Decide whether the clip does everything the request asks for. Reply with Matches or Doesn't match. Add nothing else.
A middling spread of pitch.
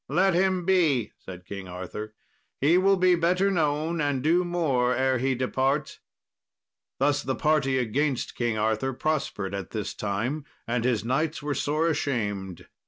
Doesn't match